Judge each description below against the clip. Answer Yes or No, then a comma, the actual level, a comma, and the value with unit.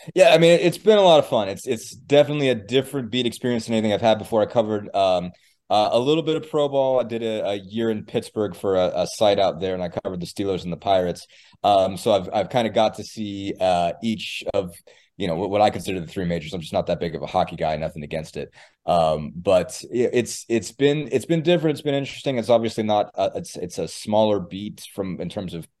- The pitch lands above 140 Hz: No, low, 110 Hz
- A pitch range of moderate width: No, wide, 6.4 semitones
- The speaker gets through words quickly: Yes, fast, 255 wpm